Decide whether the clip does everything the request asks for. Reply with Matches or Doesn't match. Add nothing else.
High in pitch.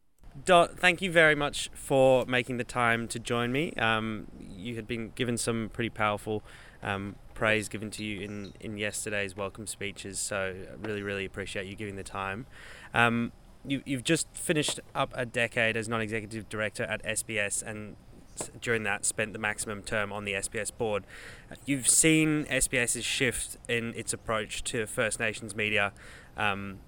Doesn't match